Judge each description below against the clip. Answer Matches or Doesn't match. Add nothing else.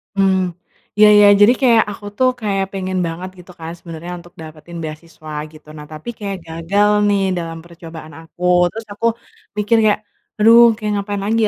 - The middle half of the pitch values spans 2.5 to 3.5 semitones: Doesn't match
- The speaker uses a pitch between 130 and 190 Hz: Matches